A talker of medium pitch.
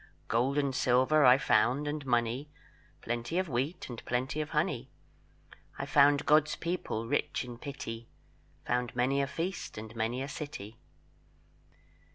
No: low, 130 Hz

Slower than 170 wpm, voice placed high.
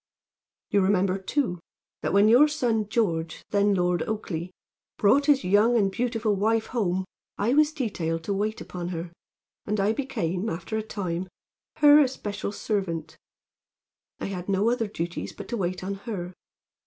Yes: average, 155 wpm; high, 200 Hz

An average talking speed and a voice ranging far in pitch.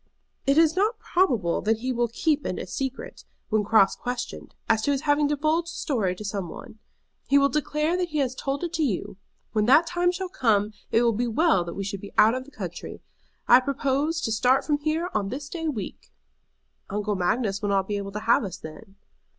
No: fast, 220 wpm; wide, 6.4 semitones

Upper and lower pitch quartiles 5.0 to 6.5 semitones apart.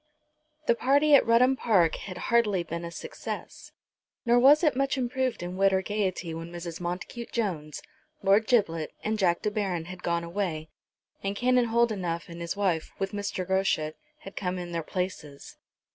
Yes: wide, 5.4 semitones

